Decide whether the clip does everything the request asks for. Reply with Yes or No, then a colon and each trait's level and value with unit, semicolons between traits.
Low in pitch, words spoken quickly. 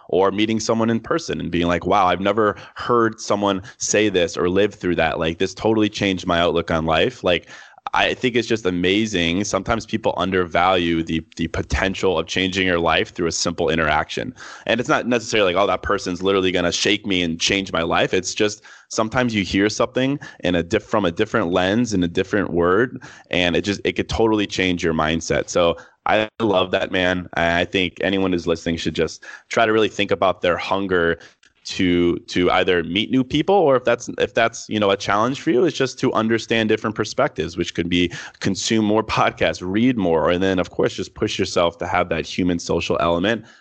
Yes: very low, 95 Hz; fast, 210 wpm